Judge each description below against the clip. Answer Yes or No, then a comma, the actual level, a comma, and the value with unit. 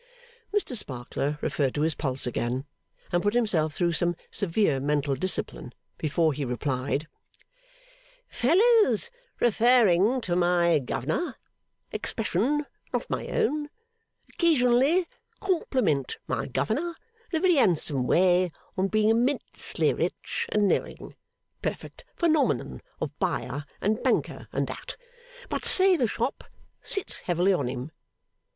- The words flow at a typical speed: No, slow, 120 wpm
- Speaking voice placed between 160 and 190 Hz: Yes, medium, 185 Hz